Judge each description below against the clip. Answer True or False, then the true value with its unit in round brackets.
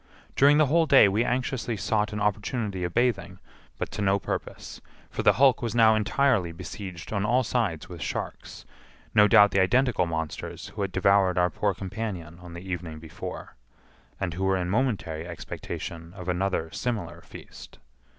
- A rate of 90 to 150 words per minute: False (170 wpm)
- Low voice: True (100 Hz)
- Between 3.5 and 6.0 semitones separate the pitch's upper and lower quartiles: True (4.2 semitones)